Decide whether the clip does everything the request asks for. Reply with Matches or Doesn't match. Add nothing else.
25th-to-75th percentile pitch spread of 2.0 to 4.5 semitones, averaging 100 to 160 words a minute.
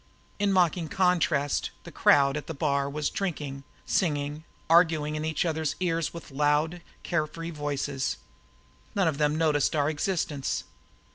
Matches